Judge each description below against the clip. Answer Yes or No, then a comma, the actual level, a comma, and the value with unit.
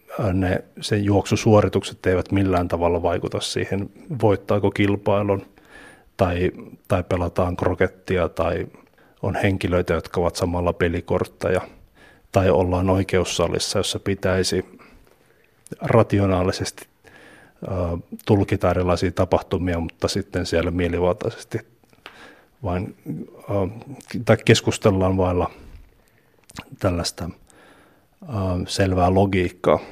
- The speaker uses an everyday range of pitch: No, narrow, 2.1 semitones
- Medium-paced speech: No, slow, 80 wpm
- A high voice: No, very low, 95 Hz